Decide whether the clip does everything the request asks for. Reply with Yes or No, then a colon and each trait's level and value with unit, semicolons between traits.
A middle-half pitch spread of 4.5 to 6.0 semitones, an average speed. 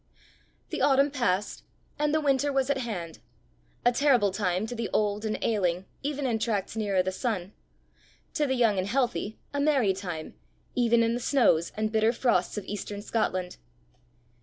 Yes: average, 5.0 semitones; average, 170 wpm